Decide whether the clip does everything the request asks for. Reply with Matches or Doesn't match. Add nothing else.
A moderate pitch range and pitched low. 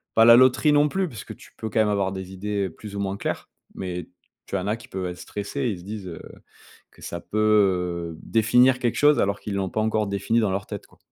Matches